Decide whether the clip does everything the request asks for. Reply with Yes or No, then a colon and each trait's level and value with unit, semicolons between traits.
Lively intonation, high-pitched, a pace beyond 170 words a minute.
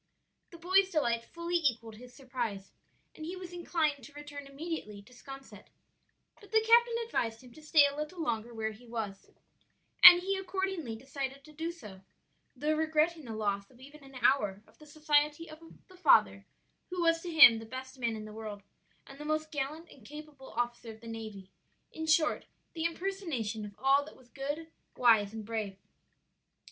Yes: wide, 6.0 semitones; very high, 280 Hz; average, 185 wpm